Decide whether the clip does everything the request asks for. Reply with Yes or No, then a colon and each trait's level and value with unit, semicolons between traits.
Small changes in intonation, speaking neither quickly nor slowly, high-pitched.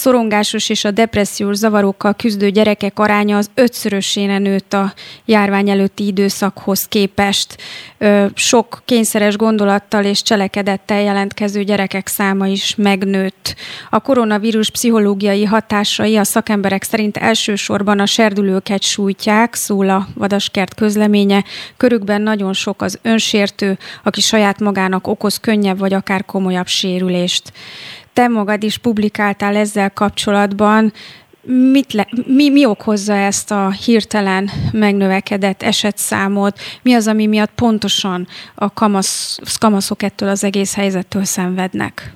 Yes: narrow, 1.5 semitones; average, 120 wpm; high, 205 Hz